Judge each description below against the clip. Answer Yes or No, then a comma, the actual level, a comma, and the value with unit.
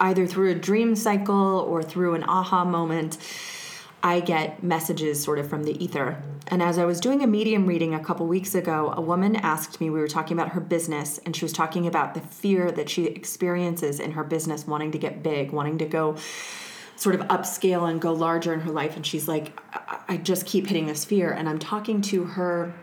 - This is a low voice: No, medium, 170 Hz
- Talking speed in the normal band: No, fast, 220 wpm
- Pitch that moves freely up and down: No, average, 2.8 semitones